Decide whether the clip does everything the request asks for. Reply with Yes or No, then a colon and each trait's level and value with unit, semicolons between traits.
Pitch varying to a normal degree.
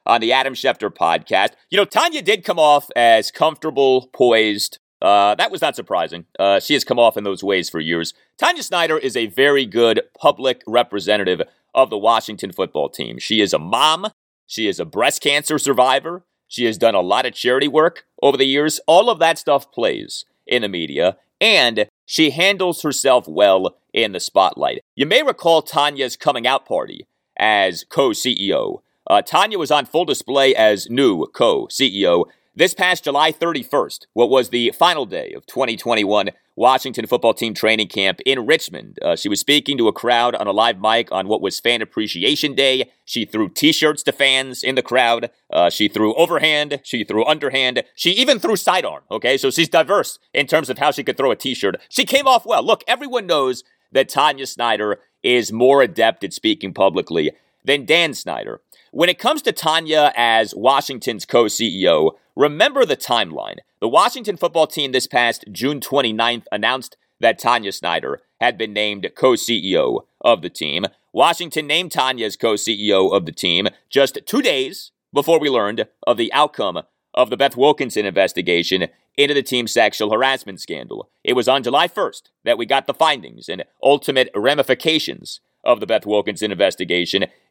No: wide, 6.3 semitones